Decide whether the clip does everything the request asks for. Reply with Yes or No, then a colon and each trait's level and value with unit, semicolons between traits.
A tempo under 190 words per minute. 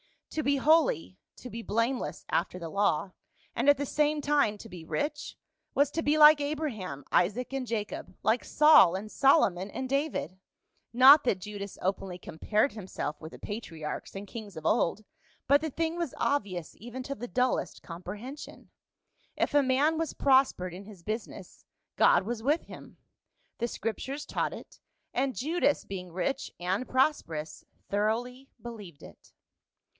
Yes: average, 165 wpm